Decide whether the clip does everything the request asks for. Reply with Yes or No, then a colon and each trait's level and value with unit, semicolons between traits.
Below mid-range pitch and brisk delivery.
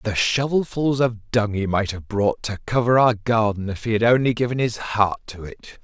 Yes: low, 110 Hz; fast, 215 wpm